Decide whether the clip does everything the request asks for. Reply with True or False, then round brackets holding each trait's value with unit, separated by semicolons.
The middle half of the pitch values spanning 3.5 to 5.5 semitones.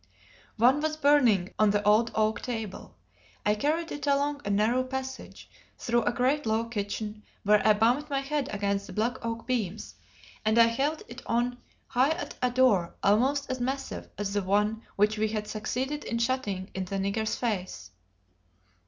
True (4.0 semitones)